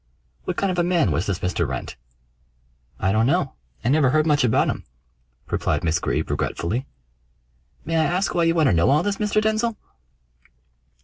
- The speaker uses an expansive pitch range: Yes, wide, 8.3 semitones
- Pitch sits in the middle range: Yes, medium, 155 Hz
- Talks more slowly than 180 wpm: No, average, 185 wpm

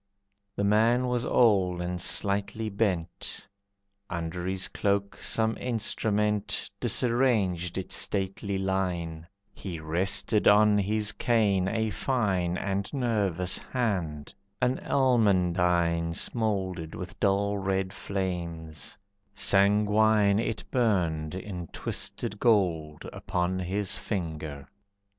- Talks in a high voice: No, low, 100 Hz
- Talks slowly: Yes, slow, 100 wpm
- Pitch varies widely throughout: No, average, 3.3 semitones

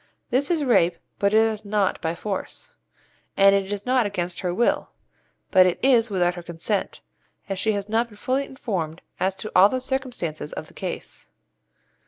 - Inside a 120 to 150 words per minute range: No, average, 185 wpm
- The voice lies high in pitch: Yes, high, 205 Hz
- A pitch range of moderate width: Yes, average, 4.7 semitones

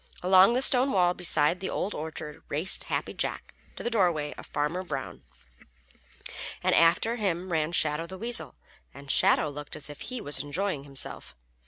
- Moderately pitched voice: Yes, medium, 170 Hz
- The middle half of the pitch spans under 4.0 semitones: No, average, 4.5 semitones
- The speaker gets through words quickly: No, average, 170 wpm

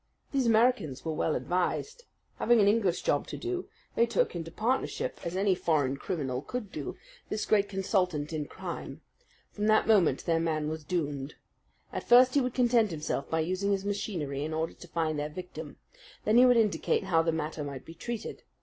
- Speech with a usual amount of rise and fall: No, wide, 5.9 semitones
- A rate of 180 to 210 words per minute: Yes, average, 190 wpm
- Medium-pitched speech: Yes, medium, 180 Hz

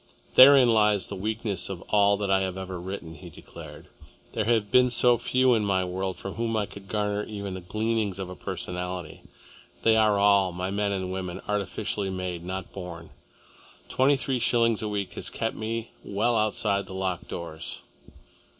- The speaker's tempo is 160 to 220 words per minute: Yes, average, 180 wpm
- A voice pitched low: Yes, low, 100 Hz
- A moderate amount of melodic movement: Yes, average, 3.0 semitones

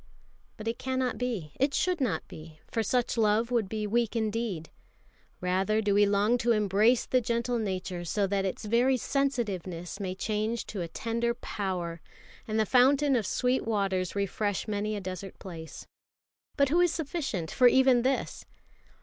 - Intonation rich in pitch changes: No, average, 4.2 semitones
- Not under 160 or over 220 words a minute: Yes, average, 165 wpm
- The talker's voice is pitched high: Yes, high, 215 Hz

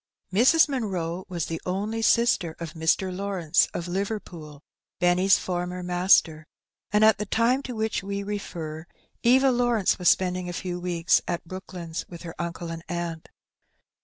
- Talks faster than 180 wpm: No, average, 160 wpm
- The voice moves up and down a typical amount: Yes, average, 3.5 semitones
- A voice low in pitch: No, medium, 180 Hz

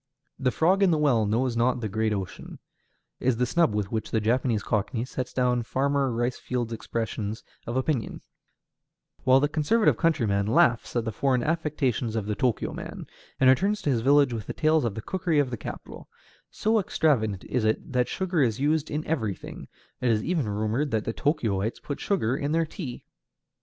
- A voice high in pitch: No, low, 125 Hz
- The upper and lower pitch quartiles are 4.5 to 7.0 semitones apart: Yes, average, 5.0 semitones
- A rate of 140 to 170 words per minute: No, average, 190 wpm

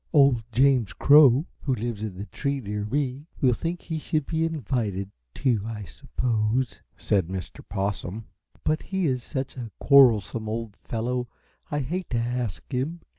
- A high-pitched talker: No, low, 125 Hz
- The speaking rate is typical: Yes, average, 160 wpm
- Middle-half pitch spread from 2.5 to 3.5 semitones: No, average, 4.6 semitones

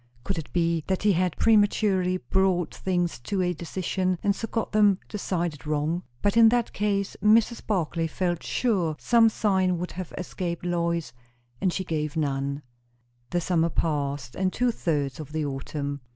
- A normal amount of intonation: Yes, average, 3.9 semitones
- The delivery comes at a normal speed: Yes, average, 165 wpm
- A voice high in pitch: No, medium, 175 Hz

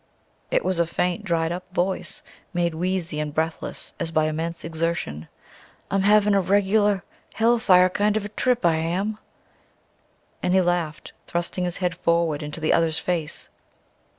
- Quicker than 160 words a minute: No, average, 155 wpm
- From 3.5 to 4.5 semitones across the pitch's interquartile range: No, average, 3.0 semitones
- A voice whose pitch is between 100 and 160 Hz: No, medium, 175 Hz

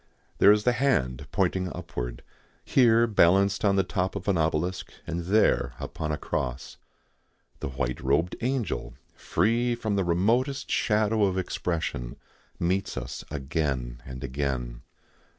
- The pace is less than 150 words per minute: Yes, slow, 135 wpm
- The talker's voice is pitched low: Yes, very low, 90 Hz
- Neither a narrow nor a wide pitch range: No, wide, 7.6 semitones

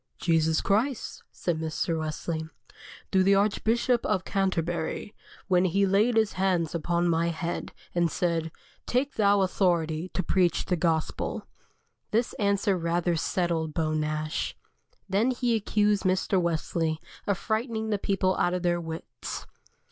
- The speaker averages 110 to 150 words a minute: Yes, average, 140 wpm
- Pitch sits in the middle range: Yes, medium, 180 Hz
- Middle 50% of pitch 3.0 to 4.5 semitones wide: Yes, average, 3.5 semitones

